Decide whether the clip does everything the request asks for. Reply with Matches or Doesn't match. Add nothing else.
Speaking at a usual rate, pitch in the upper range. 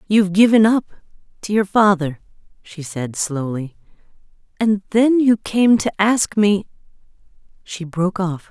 Doesn't match